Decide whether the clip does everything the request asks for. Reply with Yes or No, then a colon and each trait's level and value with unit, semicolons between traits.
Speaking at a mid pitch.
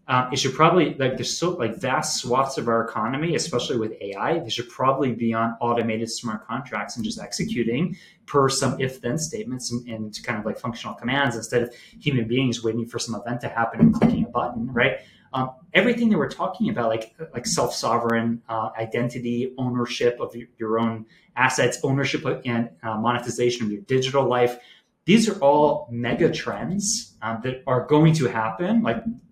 No: low, 125 Hz